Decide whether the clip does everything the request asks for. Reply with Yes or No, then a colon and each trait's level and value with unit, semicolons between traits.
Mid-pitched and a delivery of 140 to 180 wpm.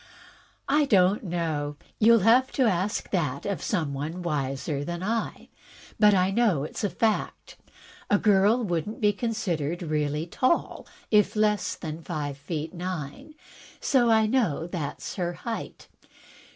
Yes: medium, 180 Hz; average, 150 wpm